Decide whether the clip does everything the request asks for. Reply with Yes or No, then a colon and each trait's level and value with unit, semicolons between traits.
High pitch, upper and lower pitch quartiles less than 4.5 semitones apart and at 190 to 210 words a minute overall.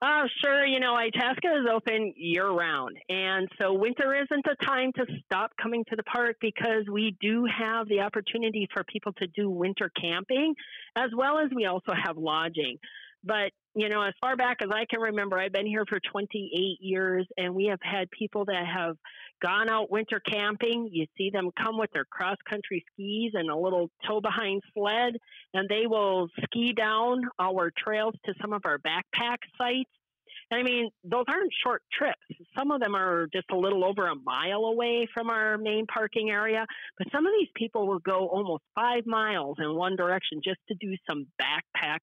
Yes: high, 215 Hz; average, 3.6 semitones; average, 195 wpm